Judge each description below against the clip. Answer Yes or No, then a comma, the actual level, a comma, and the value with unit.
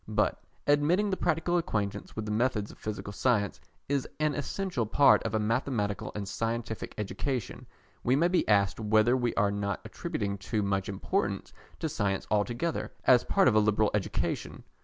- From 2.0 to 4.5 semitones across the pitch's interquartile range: No, average, 5.1 semitones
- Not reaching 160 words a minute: No, average, 175 wpm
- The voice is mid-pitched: No, low, 110 Hz